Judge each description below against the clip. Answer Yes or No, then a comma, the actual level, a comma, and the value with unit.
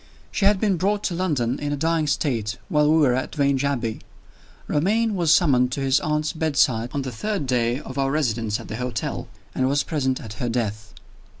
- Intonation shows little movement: No, average, 4.3 semitones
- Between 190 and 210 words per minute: Yes, fast, 205 wpm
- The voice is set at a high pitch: No, medium, 140 Hz